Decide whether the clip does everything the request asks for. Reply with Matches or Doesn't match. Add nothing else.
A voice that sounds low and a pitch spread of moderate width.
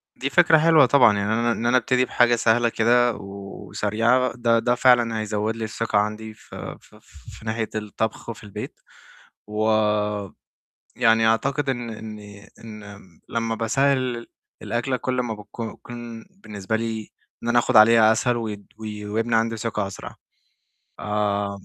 Doesn't match